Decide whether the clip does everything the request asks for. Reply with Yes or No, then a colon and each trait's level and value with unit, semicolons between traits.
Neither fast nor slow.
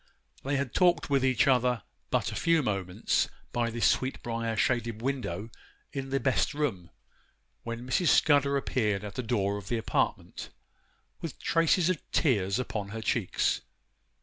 Yes: average, 150 wpm